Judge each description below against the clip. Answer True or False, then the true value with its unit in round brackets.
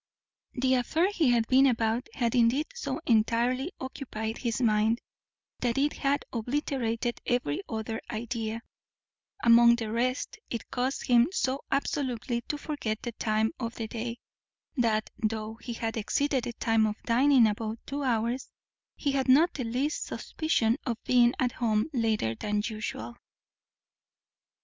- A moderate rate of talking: True (145 wpm)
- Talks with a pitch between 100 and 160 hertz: False (235 Hz)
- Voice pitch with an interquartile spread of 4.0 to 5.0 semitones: False (2.8 semitones)